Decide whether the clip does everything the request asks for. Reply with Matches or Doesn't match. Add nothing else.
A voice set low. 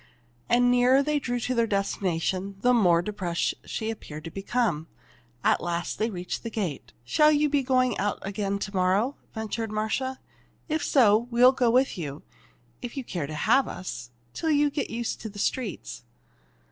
Doesn't match